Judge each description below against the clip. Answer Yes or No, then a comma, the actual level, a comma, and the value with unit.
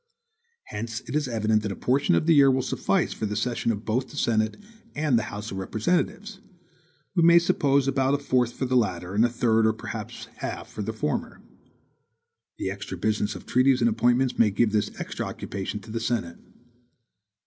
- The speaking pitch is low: Yes, low, 115 Hz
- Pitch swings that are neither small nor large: Yes, average, 3.8 semitones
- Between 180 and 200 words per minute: Yes, average, 195 wpm